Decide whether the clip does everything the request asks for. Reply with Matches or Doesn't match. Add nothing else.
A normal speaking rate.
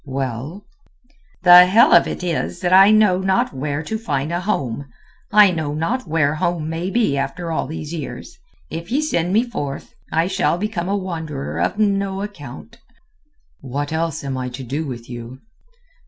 Matches